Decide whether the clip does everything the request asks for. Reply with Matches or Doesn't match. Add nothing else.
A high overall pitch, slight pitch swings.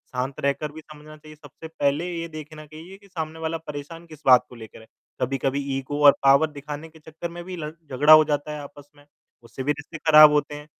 Doesn't match